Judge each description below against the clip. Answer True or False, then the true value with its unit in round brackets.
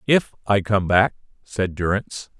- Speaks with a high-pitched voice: False (105 Hz)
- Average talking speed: True (150 wpm)